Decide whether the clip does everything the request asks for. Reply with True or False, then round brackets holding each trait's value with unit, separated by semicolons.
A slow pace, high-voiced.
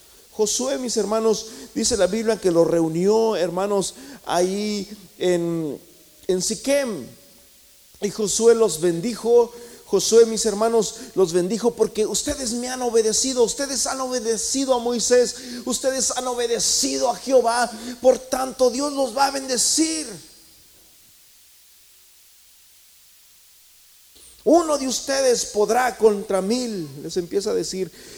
True (115 wpm; 230 Hz)